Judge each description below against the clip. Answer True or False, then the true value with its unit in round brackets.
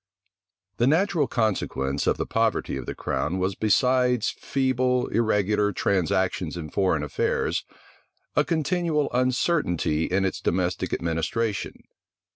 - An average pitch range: False (6.0 semitones)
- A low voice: True (105 Hz)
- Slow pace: True (115 wpm)